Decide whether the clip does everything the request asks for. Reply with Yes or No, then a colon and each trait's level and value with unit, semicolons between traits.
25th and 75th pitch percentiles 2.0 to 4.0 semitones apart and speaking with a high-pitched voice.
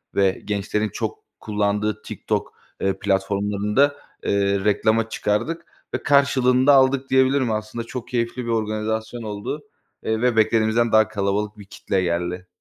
No: average, 3.1 semitones; low, 110 Hz